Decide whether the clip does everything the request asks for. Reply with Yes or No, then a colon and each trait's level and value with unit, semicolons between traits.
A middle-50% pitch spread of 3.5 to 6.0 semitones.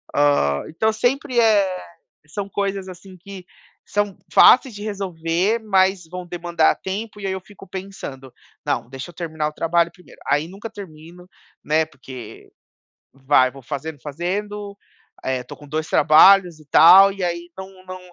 Yes: average, 4.2 semitones